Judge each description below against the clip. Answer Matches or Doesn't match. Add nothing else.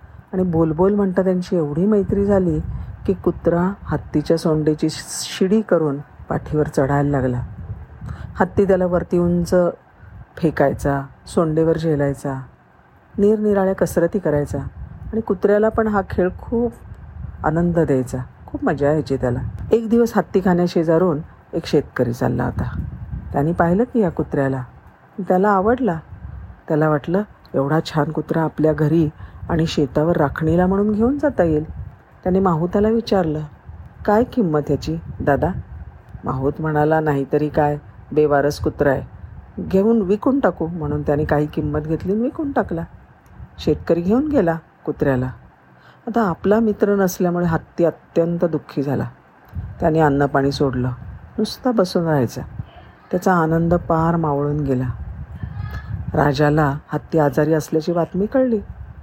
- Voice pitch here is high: Doesn't match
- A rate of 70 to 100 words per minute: Doesn't match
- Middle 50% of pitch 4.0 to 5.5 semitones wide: Matches